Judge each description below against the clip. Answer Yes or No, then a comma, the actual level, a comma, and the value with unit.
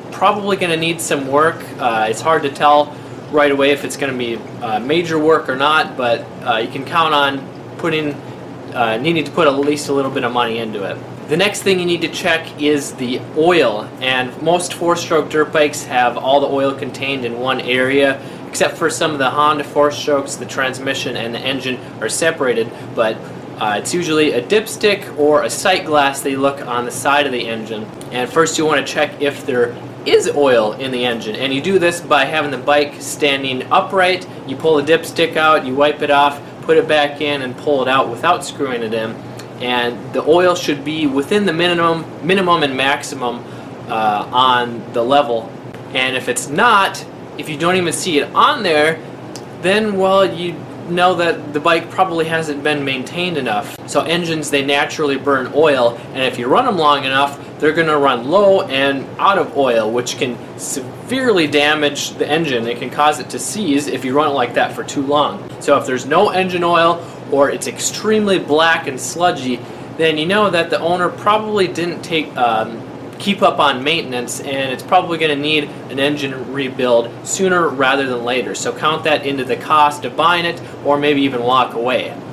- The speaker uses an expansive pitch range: No, average, 3.6 semitones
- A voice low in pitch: No, medium, 145 Hz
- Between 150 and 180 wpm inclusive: No, fast, 205 wpm